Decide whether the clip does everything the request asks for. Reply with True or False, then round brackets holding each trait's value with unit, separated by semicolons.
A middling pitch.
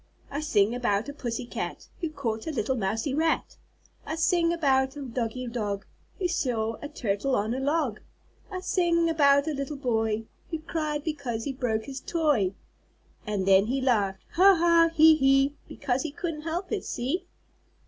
False (275 Hz)